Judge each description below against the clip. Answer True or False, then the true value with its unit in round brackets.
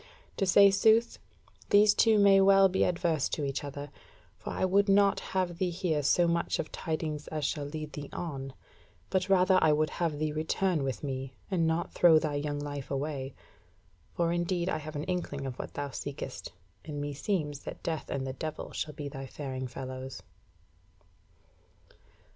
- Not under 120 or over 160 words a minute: False (175 wpm)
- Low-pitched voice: False (155 Hz)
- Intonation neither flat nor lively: True (4.2 semitones)